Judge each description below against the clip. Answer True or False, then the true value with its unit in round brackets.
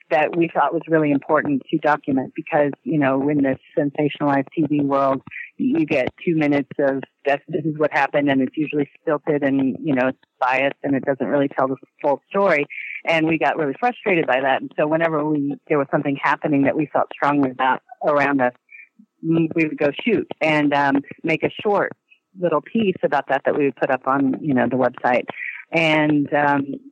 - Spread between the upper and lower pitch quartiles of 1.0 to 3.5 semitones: True (2.6 semitones)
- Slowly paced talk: False (200 wpm)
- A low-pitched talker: False (145 Hz)